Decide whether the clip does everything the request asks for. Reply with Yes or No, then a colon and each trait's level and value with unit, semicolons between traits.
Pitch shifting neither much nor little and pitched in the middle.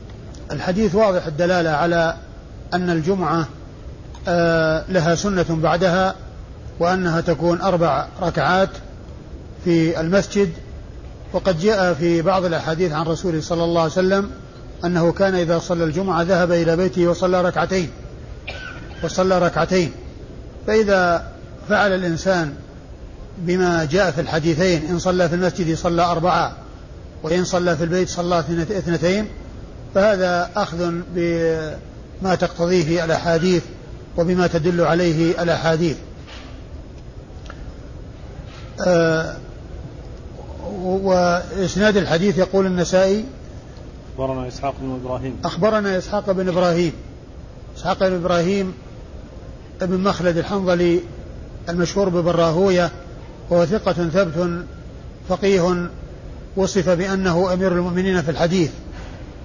No: narrow, 1.8 semitones; medium, 175 Hz